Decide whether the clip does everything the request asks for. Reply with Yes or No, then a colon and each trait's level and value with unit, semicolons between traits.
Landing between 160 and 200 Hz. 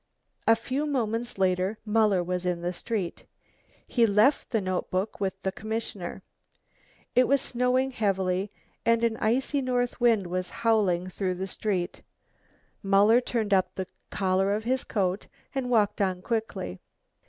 No: high, 210 Hz